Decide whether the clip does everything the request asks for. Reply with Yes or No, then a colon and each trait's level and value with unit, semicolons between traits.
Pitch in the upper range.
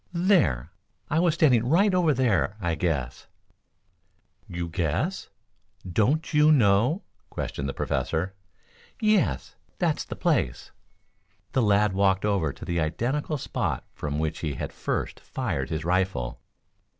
No: low, 100 Hz